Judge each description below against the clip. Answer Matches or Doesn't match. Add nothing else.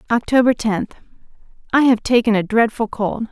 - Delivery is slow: Matches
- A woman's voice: Matches